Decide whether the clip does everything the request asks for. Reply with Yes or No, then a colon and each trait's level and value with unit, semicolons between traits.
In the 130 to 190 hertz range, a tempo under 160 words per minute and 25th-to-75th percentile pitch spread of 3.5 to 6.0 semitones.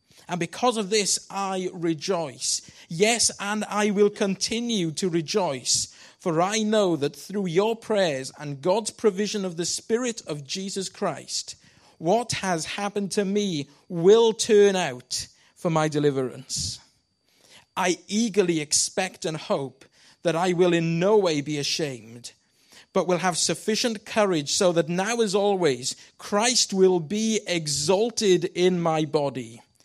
Yes: medium, 185 Hz; average, 140 wpm; average, 4.8 semitones